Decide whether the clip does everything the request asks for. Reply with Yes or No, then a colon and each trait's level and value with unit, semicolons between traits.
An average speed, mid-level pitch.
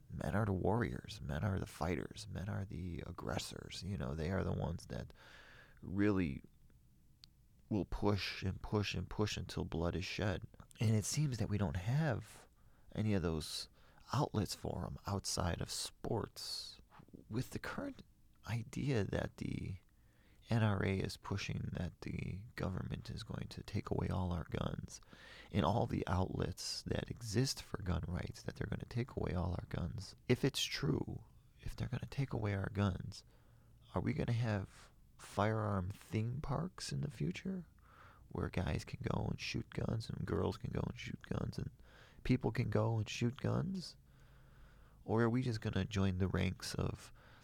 No: average, 175 wpm; low, 105 Hz